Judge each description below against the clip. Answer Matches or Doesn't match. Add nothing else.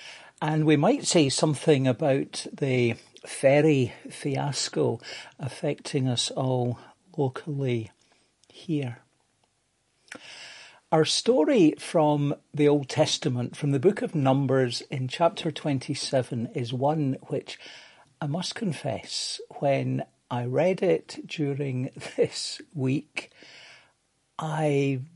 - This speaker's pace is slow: Matches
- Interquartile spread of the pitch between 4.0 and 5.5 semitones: Doesn't match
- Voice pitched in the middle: Matches